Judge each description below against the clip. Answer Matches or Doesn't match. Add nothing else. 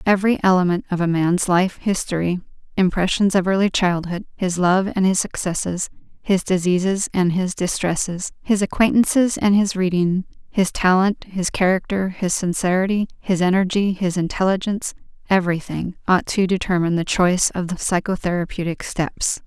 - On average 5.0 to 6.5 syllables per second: Matches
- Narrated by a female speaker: Matches